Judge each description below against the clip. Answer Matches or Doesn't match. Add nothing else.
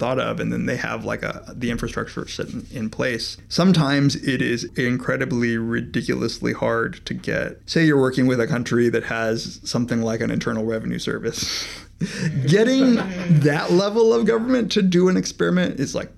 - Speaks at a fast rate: Doesn't match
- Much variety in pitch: Matches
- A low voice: Matches